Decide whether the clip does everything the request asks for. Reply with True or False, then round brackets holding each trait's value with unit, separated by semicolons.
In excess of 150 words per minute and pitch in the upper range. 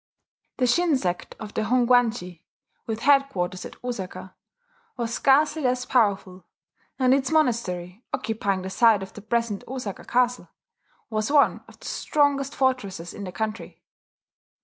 False (140 wpm; 230 Hz)